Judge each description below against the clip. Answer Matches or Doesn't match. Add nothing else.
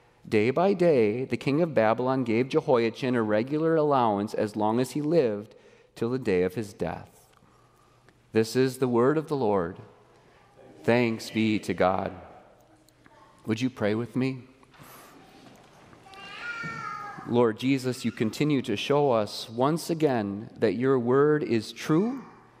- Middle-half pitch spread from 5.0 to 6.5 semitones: Doesn't match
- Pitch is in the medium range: Doesn't match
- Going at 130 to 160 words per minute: Matches